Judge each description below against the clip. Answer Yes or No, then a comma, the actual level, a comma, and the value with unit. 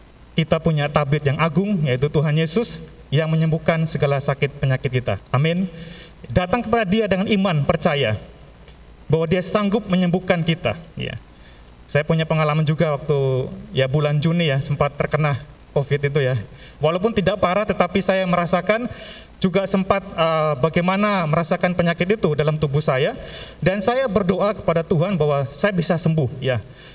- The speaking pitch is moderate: Yes, medium, 160 Hz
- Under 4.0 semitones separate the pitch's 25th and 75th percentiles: No, average, 4.4 semitones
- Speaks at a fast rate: Yes, fast, 150 wpm